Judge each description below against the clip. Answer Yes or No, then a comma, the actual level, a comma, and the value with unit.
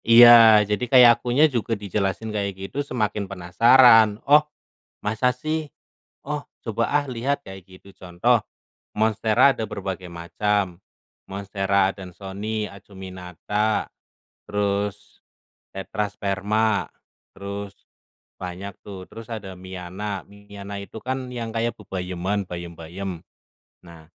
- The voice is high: No, low, 100 Hz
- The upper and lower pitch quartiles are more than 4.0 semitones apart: No, average, 3.0 semitones